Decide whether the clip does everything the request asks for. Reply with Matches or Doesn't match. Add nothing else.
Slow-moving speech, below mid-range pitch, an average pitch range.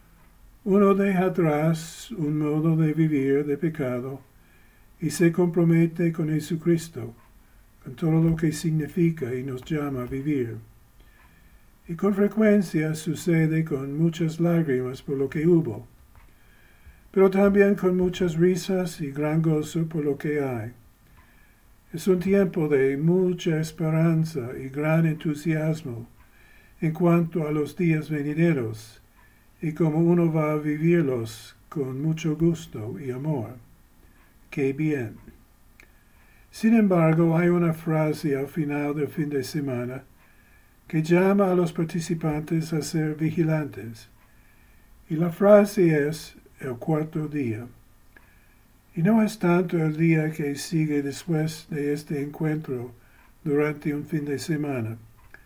Doesn't match